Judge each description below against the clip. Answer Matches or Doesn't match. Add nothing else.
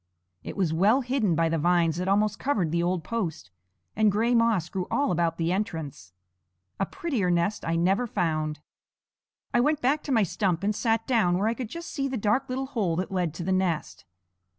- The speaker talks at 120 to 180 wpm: Doesn't match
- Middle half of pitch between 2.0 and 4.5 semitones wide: Doesn't match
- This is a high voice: Matches